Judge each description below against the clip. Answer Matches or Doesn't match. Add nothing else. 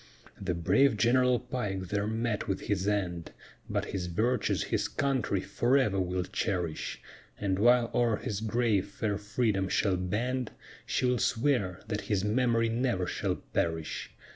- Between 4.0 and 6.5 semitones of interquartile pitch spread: Matches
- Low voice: Matches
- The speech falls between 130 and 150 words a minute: Matches